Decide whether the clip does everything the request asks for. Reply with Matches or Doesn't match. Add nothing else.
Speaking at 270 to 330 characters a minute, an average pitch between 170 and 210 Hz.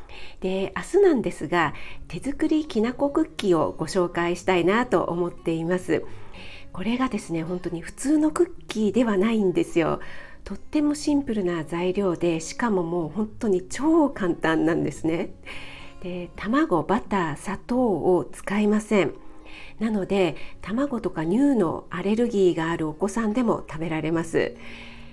Matches